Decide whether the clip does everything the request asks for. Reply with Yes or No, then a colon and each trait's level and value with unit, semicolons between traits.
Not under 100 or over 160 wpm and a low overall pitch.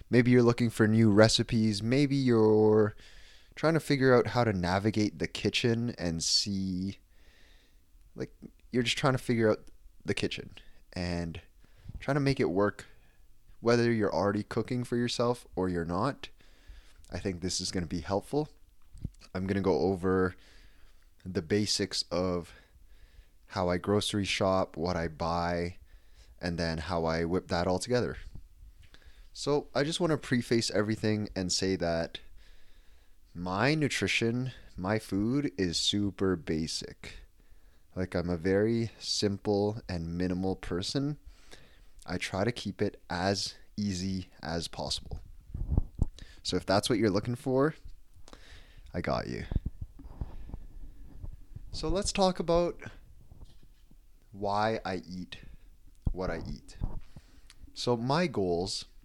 Yes: slow, 135 wpm; very low, 95 Hz